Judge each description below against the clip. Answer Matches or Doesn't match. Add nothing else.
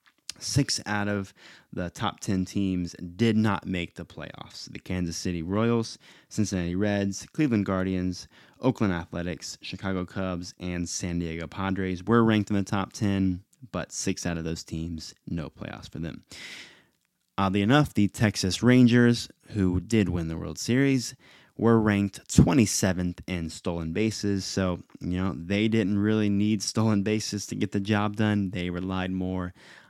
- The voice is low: Matches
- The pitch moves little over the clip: Doesn't match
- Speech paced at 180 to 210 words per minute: Doesn't match